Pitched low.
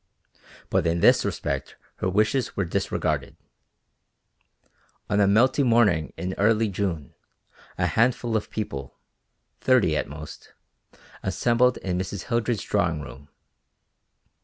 Yes: low, 100 Hz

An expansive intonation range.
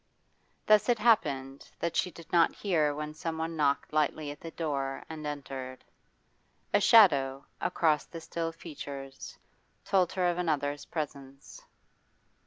No: average, 3.3 semitones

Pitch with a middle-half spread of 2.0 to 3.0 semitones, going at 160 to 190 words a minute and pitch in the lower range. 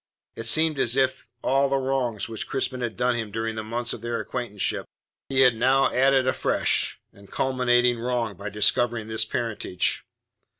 Yes: average, 2.7 semitones; average, 180 wpm; low, 120 Hz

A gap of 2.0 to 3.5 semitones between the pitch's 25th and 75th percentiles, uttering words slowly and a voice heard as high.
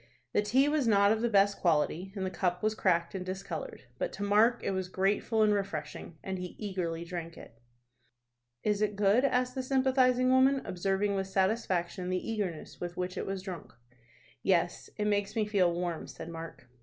No: average, 3.2 semitones; average, 190 wpm; high, 195 Hz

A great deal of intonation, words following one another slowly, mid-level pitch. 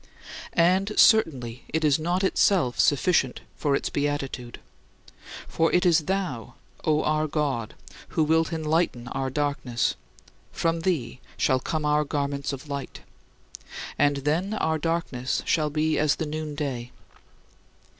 No: average, 3.0 semitones; slow, 130 wpm; medium, 150 Hz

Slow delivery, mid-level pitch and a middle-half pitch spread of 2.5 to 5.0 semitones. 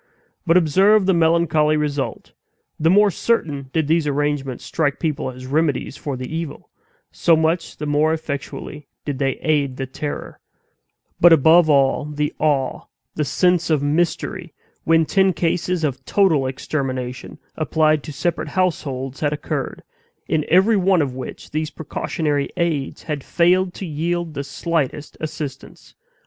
No: average, 145 wpm; medium, 155 Hz; average, 3.0 semitones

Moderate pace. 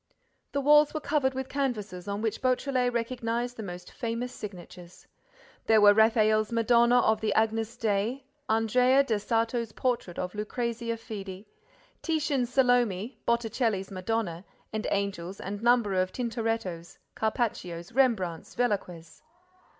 No: slow, 125 wpm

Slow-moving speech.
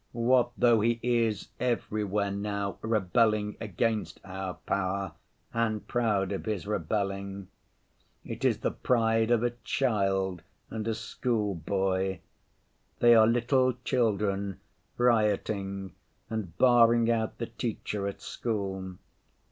Yes: slow, 115 wpm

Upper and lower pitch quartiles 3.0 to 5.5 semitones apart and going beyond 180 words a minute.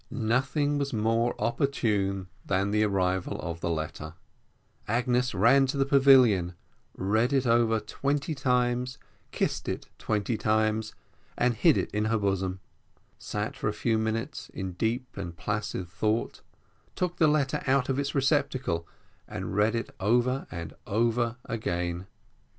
No: average, 4.6 semitones; average, 145 wpm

